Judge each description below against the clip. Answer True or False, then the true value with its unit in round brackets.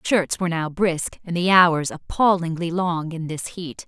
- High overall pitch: False (170 Hz)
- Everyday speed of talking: True (185 wpm)